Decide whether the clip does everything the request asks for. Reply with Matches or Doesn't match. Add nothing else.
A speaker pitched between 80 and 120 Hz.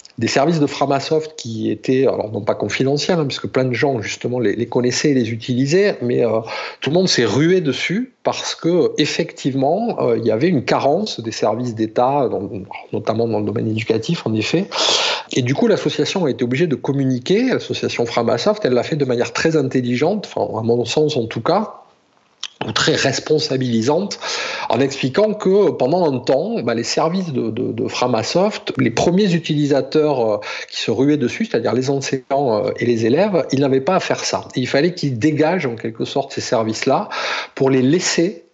Doesn't match